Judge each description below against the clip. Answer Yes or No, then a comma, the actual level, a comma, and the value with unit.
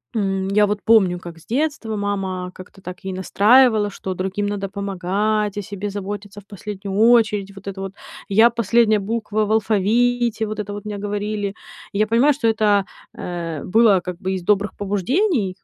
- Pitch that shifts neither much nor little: No, narrow, 2.1 semitones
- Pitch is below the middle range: No, high, 205 Hz